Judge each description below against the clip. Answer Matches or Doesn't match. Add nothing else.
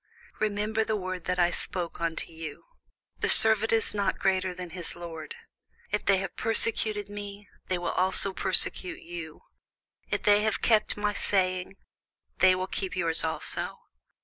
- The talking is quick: Doesn't match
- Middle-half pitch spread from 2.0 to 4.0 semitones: Matches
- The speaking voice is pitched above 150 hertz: Matches